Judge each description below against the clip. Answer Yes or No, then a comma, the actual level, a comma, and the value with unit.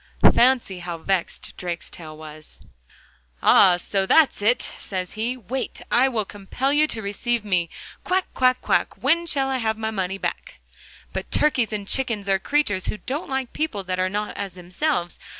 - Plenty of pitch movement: Yes, wide, 5.8 semitones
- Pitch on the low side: No, high, 210 Hz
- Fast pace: No, average, 170 wpm